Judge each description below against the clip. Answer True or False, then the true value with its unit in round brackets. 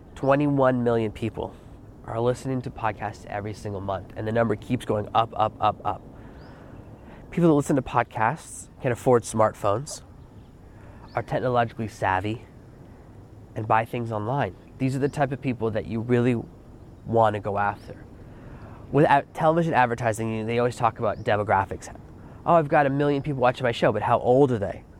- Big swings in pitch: False (3.2 semitones)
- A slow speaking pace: False (165 wpm)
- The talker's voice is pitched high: False (115 Hz)